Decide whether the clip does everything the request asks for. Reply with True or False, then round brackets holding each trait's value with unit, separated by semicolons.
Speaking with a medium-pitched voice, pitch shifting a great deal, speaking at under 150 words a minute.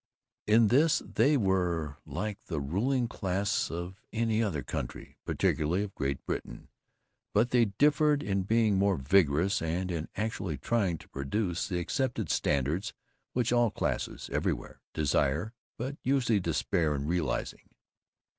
False (95 Hz; 6.0 semitones; 135 wpm)